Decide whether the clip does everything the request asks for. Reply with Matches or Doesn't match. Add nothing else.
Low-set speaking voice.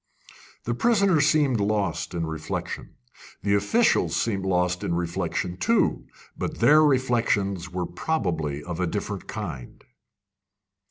Matches